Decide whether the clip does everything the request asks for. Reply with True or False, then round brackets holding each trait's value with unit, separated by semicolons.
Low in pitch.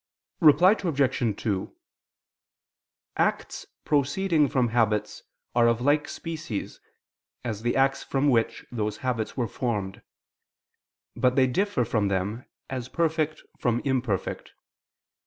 True (125 Hz)